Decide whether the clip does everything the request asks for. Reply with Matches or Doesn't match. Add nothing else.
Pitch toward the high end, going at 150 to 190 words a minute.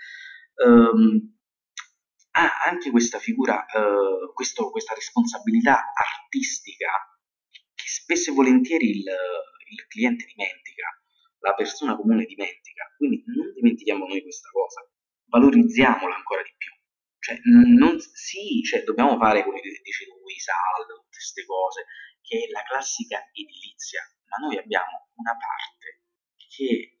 Doesn't match